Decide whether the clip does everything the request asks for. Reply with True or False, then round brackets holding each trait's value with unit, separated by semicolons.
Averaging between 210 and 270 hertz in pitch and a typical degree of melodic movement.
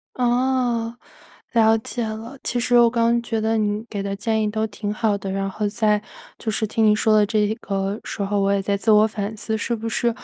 False (220 Hz; 1.9 semitones)